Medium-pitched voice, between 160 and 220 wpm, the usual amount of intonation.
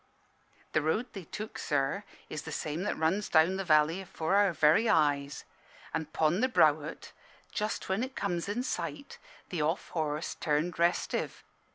Yes: medium, 170 Hz; average, 170 wpm; average, 4.5 semitones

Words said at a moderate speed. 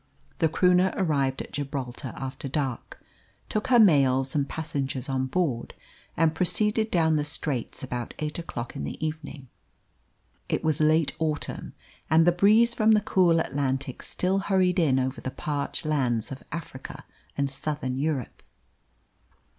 Yes: average, 145 wpm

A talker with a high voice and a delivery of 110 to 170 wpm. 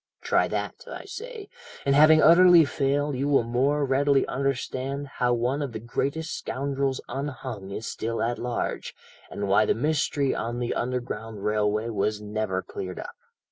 No: low, 130 Hz; average, 160 wpm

